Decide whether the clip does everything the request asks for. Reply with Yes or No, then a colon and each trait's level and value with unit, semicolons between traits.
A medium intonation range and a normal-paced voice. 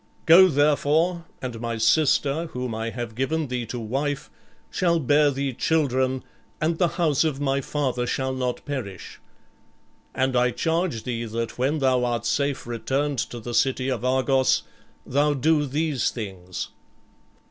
Yes: average, 3.3 semitones; average, 150 wpm